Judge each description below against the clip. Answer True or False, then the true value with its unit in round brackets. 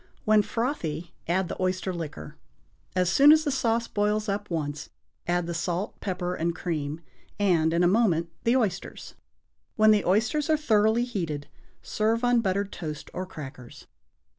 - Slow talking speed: False (160 wpm)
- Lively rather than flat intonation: False (4.6 semitones)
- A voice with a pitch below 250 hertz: True (185 Hz)